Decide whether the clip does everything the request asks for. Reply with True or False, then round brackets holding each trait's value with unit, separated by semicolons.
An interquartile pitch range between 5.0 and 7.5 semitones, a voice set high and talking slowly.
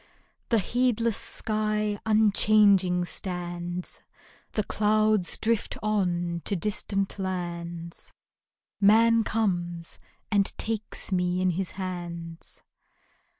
False (3.4 semitones; 195 Hz; 90 wpm)